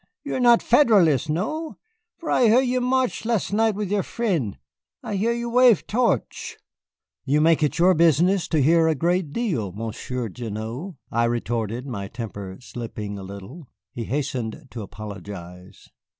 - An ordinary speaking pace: Yes, average, 160 wpm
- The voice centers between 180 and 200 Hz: No, medium, 150 Hz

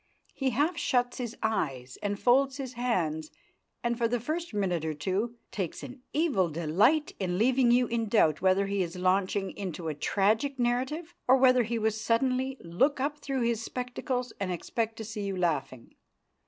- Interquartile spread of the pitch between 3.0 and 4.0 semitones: No, average, 5.3 semitones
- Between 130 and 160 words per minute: No, average, 180 wpm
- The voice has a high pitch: Yes, high, 230 Hz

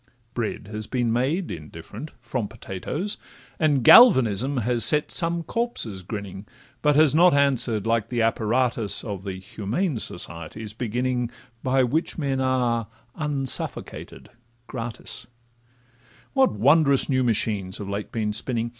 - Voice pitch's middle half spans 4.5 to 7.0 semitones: Yes, average, 4.8 semitones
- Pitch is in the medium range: No, low, 120 Hz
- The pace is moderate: No, slow, 130 wpm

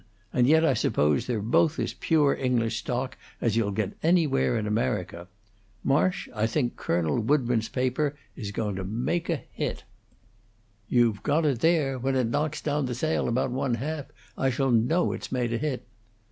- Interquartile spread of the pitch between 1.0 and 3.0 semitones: No, average, 4.5 semitones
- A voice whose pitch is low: Yes, low, 125 Hz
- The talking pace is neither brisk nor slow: Yes, average, 175 wpm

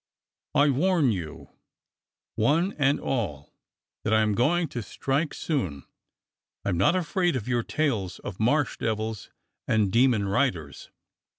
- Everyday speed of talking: No, slow, 125 wpm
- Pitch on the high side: No, low, 120 Hz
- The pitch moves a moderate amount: No, wide, 6.4 semitones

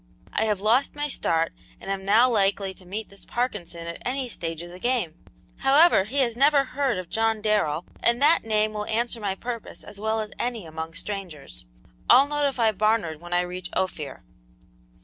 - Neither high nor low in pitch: No, high, 215 Hz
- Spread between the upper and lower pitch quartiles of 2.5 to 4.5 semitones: No, average, 5.0 semitones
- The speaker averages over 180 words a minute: Yes, average, 190 wpm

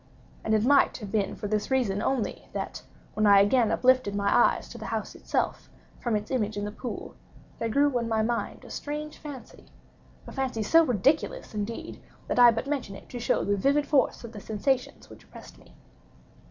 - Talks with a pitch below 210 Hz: No, high, 235 Hz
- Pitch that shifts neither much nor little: Yes, average, 4.2 semitones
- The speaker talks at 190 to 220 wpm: Yes, average, 195 wpm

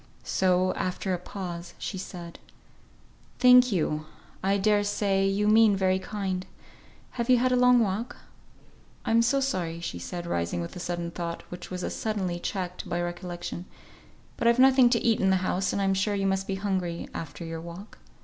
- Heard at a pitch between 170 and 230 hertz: Yes, high, 190 Hz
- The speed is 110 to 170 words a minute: No, average, 185 wpm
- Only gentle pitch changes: No, average, 3.4 semitones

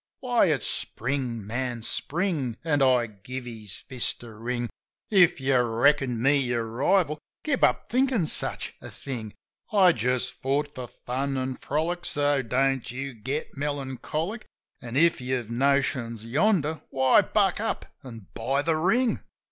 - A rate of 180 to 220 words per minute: No, average, 150 wpm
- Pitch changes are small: No, average, 4.4 semitones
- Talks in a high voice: No, low, 135 Hz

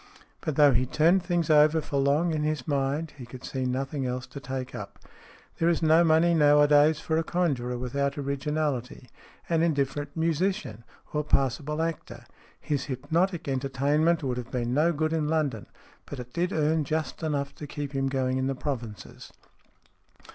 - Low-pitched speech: No, medium, 145 Hz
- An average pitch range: Yes, average, 3.2 semitones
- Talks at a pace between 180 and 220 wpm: No, average, 170 wpm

